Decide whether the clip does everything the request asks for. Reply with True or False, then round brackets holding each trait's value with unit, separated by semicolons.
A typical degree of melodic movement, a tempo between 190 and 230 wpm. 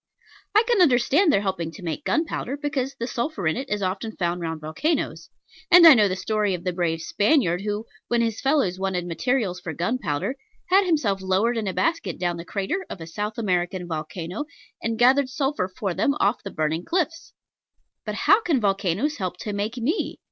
False (7.2 semitones; 195 wpm)